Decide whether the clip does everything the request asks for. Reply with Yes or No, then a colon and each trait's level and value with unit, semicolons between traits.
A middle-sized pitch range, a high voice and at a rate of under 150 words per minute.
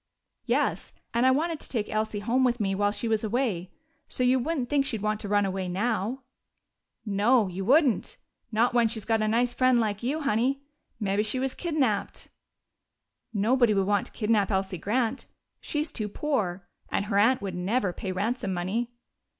No: average, 4.0 semitones; high, 220 Hz; average, 185 wpm